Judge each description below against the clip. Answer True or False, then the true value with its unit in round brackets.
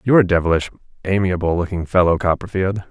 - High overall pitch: False (90 Hz)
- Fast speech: False (145 wpm)